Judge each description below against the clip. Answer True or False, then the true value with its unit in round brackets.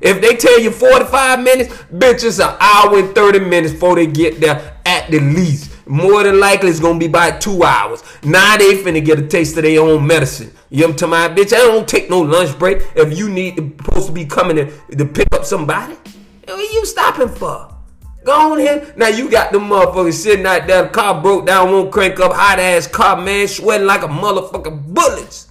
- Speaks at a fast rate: True (220 wpm)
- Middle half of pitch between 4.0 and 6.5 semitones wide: True (4.9 semitones)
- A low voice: False (190 Hz)